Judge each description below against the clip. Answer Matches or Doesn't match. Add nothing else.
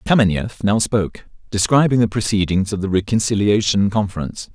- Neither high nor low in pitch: Doesn't match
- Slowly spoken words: Matches